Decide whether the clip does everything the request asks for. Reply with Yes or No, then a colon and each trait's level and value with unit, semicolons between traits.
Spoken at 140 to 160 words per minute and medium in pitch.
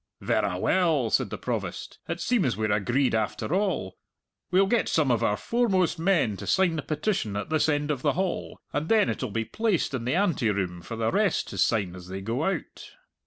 No: fast, 205 wpm; medium, 145 Hz